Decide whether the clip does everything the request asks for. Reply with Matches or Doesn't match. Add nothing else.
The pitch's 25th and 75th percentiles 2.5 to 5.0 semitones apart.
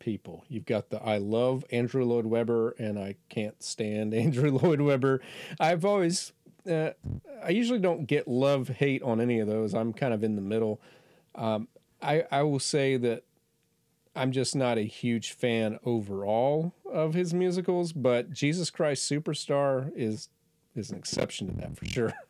Doesn't match